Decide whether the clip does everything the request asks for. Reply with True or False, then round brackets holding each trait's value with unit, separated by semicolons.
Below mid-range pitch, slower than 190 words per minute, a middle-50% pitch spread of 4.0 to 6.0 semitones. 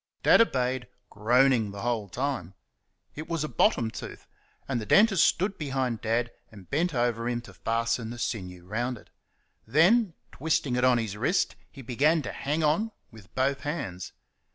True (125 Hz; 170 wpm; 4.8 semitones)